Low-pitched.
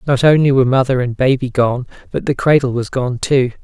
Yes: low, 130 Hz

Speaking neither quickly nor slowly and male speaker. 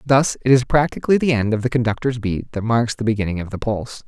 No: fast, 250 wpm; male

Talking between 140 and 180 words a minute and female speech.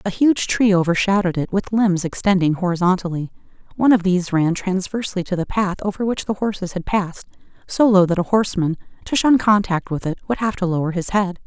No: average, 200 wpm; female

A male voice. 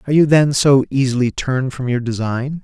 Yes: male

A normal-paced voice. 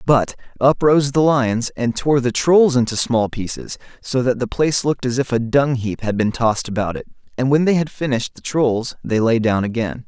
No: fast, 225 wpm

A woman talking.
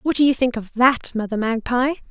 Yes: female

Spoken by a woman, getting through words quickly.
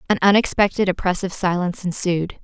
No: female; slow, 125 wpm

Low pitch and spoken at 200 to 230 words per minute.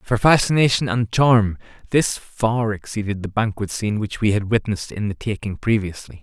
No: low, 110 Hz; average, 175 wpm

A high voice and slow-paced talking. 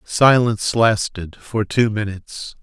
No: low, 110 Hz; slow, 115 wpm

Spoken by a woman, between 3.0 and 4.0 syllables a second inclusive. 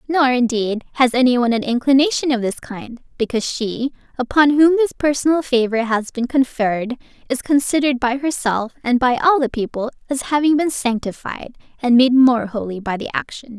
No: female; 5.4 syllables/s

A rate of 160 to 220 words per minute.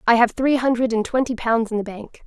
No: fast, 265 wpm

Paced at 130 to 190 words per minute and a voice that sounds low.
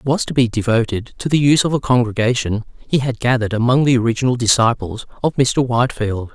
No: average, 200 wpm; low, 120 Hz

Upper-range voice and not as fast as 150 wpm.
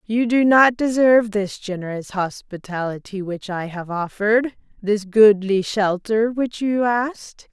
Yes: high, 210 Hz; slow, 135 wpm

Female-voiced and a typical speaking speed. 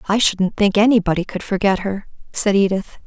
Yes: female; average, 175 wpm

